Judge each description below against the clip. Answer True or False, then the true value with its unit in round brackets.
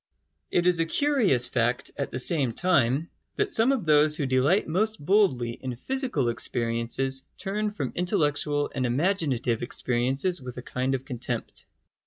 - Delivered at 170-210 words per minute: False (155 wpm)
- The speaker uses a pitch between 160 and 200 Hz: False (140 Hz)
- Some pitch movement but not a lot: False (6.6 semitones)